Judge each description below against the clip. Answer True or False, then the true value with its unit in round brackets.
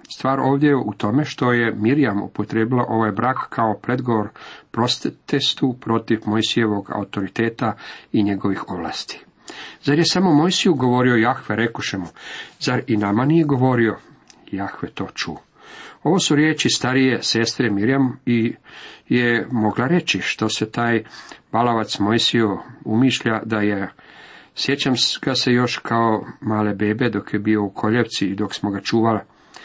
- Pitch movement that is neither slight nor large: True (3.3 semitones)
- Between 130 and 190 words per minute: True (145 wpm)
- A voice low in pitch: True (115 Hz)